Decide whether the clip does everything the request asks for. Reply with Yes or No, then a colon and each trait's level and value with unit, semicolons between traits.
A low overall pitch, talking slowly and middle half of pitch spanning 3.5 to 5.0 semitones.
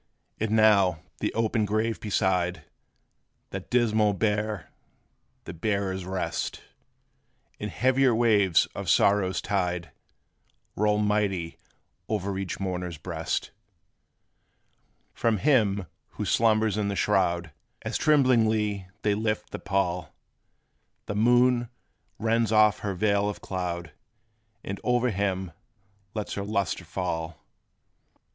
No: low, 100 Hz; slow, 110 wpm; average, 2.9 semitones